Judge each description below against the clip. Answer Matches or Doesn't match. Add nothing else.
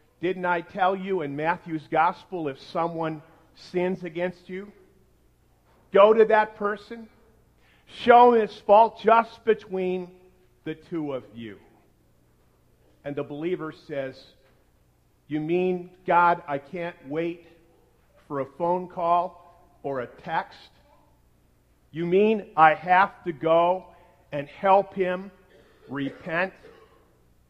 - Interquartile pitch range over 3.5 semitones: Matches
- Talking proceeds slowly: Matches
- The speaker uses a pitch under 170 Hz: Doesn't match